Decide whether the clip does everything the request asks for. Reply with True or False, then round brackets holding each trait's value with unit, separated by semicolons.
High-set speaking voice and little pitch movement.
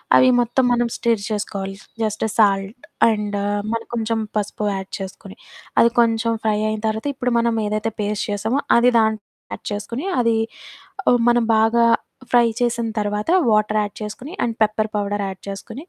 True (220 Hz; 2.1 semitones)